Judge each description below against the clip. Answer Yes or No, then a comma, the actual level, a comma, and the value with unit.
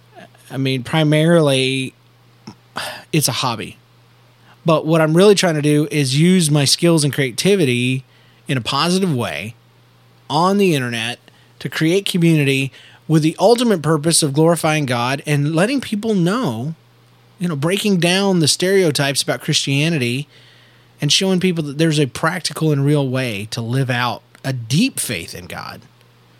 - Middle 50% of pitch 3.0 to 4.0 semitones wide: No, average, 5.0 semitones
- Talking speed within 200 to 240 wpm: No, average, 150 wpm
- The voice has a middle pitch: Yes, medium, 150 Hz